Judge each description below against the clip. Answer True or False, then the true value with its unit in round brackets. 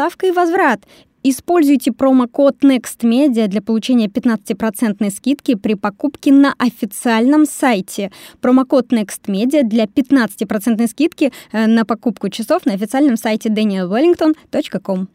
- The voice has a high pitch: True (245 Hz)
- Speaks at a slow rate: True (105 wpm)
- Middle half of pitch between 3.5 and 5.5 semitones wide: True (4.3 semitones)